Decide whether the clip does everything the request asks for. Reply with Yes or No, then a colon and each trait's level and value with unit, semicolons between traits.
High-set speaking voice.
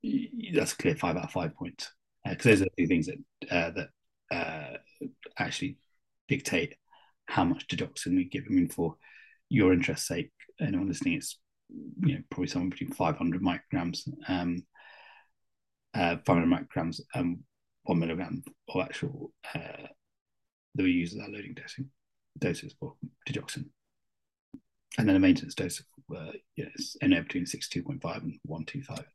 Yes: very high, 250 Hz